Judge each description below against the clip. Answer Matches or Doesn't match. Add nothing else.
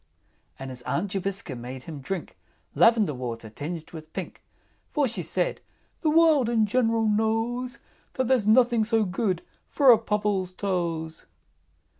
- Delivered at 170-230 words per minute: Doesn't match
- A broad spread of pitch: Matches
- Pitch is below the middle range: Doesn't match